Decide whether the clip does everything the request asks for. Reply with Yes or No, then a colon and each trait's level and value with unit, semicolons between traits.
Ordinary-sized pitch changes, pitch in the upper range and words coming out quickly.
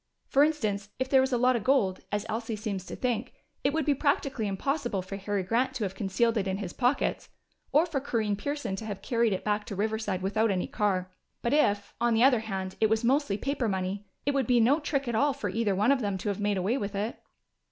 Yes: average, 4.5 semitones; high, 220 Hz; fast, 245 wpm